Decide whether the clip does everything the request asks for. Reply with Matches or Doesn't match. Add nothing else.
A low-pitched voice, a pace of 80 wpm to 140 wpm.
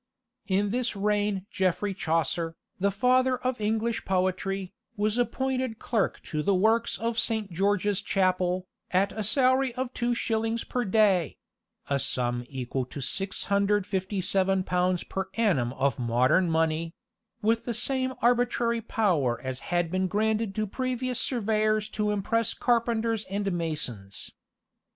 Doesn't match